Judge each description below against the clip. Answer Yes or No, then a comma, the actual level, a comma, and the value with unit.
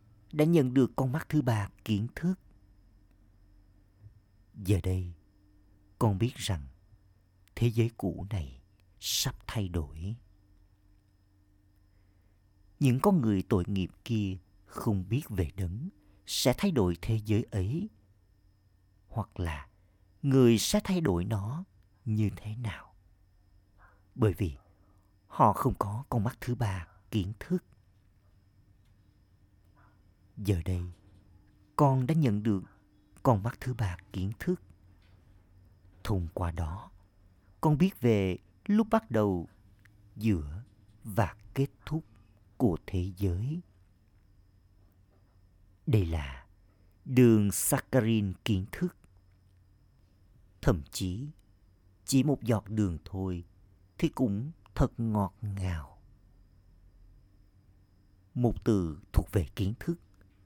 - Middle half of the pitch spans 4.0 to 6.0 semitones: No, narrow, 2.6 semitones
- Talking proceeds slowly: Yes, slow, 110 wpm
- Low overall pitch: Yes, low, 100 Hz